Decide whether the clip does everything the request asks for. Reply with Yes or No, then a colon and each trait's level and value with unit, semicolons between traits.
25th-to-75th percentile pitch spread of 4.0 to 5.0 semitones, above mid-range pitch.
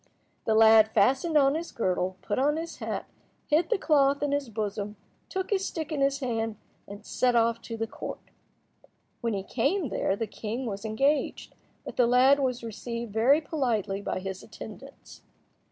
Yes: average, 4.6 semitones; high, 235 Hz